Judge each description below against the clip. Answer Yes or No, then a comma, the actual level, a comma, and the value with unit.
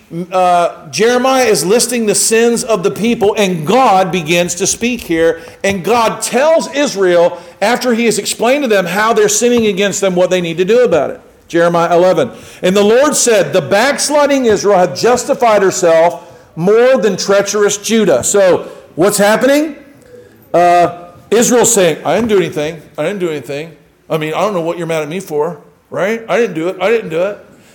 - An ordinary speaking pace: Yes, average, 190 wpm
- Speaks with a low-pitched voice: No, high, 200 Hz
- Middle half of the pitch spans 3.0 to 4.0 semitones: No, average, 5.2 semitones